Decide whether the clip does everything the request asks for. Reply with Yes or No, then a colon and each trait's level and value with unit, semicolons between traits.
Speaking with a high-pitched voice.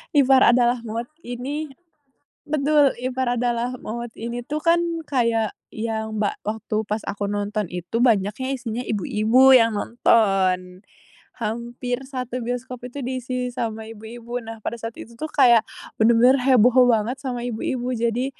Yes: high, 235 Hz